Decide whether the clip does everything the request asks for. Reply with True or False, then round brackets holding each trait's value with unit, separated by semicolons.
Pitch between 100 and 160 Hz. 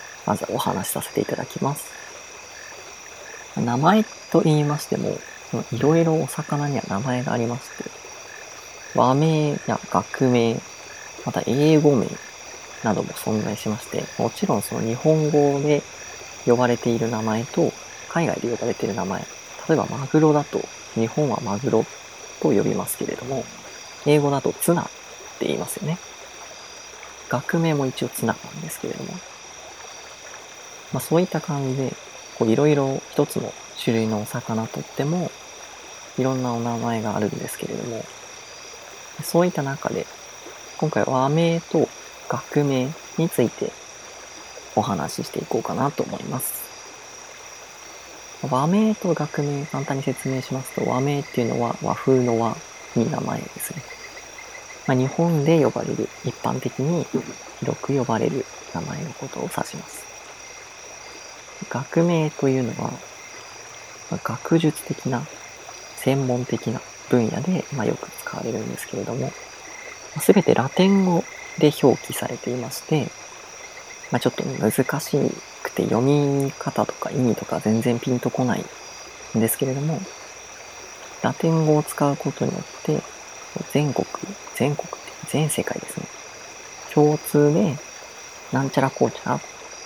True (140 Hz)